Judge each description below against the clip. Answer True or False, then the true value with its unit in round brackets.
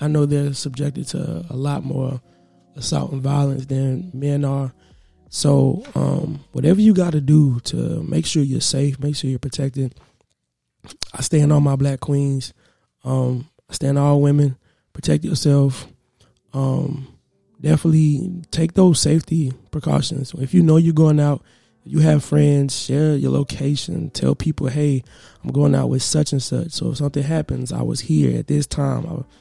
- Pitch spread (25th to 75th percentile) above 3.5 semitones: False (2.4 semitones)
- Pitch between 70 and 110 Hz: False (140 Hz)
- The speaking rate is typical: True (170 wpm)